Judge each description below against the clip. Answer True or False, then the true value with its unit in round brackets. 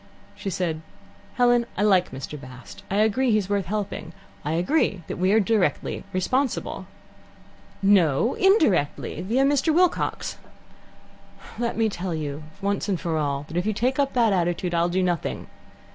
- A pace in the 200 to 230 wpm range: False (160 wpm)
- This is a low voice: False (195 Hz)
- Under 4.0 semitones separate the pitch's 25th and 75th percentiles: False (5.5 semitones)